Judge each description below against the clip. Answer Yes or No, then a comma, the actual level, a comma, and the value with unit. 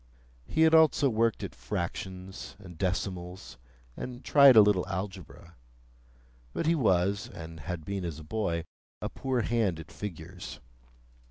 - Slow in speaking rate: No, average, 145 wpm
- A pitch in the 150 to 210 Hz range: No, very low, 95 Hz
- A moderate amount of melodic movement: Yes, average, 4.8 semitones